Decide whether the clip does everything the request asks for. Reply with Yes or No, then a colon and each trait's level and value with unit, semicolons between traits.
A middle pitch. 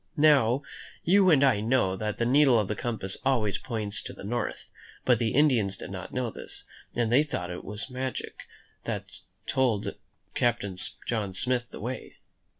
No: low, 120 Hz